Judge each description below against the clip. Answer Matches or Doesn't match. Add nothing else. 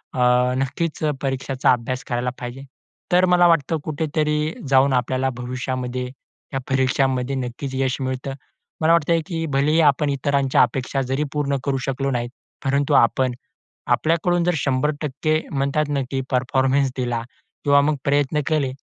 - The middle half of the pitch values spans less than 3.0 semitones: Matches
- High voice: Doesn't match